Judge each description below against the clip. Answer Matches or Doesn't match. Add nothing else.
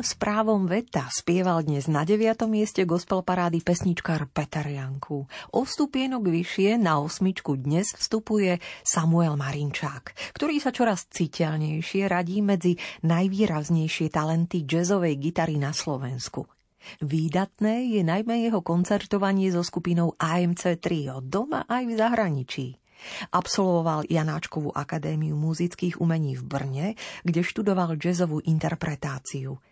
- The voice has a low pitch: Doesn't match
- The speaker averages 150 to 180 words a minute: Doesn't match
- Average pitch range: Matches